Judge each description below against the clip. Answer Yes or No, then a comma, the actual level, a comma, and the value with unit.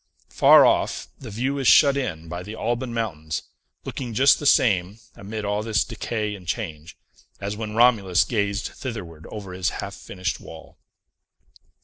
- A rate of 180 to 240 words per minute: No, average, 155 wpm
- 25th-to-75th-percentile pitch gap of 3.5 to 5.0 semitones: Yes, average, 4.4 semitones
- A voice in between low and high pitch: No, low, 105 Hz